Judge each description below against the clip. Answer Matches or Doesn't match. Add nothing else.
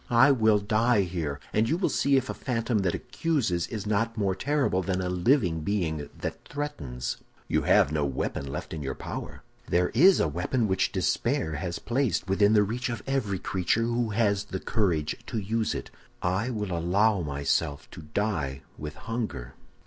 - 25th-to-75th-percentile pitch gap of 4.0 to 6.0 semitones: Matches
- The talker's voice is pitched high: Doesn't match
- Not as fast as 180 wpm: Doesn't match